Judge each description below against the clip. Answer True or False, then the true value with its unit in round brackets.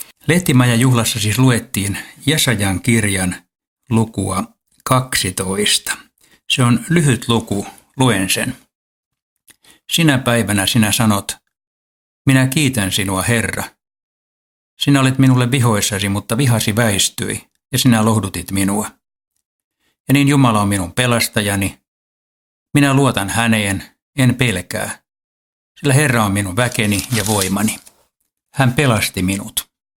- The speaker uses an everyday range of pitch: True (4.5 semitones)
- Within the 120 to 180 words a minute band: False (110 wpm)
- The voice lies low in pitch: True (115 Hz)